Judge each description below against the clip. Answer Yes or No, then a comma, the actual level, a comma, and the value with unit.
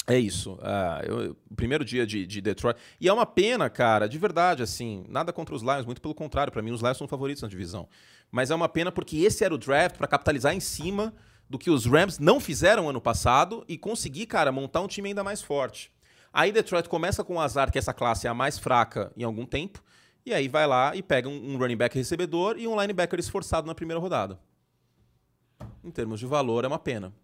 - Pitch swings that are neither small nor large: No, wide, 6.6 semitones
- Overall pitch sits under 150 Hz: Yes, medium, 140 Hz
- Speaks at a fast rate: Yes, fast, 230 wpm